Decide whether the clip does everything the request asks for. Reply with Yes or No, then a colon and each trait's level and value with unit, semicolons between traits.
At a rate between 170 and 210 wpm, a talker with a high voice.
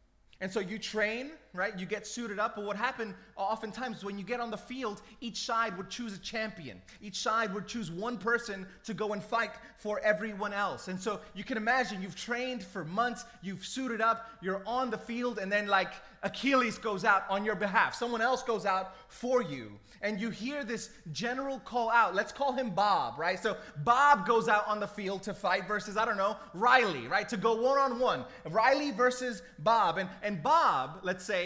Yes: fast, 205 wpm; high, 215 Hz